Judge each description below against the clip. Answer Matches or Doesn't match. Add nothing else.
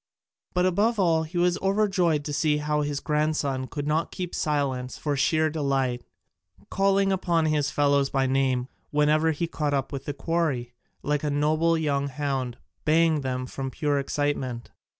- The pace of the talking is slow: Doesn't match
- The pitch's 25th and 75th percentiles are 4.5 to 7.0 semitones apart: Doesn't match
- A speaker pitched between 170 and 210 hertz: Doesn't match